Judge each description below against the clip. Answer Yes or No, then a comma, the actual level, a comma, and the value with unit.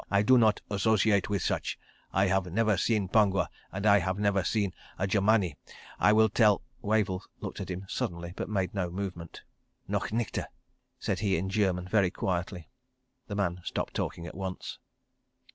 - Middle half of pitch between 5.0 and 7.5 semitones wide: No, narrow, 2.5 semitones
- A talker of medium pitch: No, low, 100 Hz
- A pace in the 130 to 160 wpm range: No, average, 175 wpm